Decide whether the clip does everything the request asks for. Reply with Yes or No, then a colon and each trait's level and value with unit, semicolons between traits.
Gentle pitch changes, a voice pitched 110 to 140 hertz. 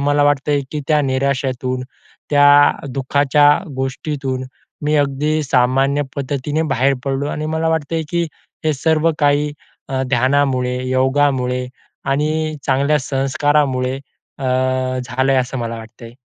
Yes: narrow, 2.1 semitones; low, 135 Hz